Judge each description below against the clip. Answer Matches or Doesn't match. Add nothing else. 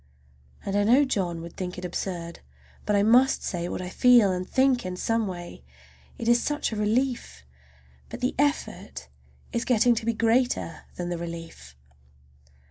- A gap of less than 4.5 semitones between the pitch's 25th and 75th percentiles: Doesn't match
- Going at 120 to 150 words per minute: Doesn't match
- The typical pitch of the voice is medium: Doesn't match